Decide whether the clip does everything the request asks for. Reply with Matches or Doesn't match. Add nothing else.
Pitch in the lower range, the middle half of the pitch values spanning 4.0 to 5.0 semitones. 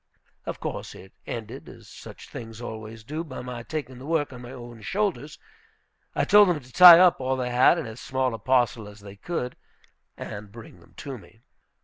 Matches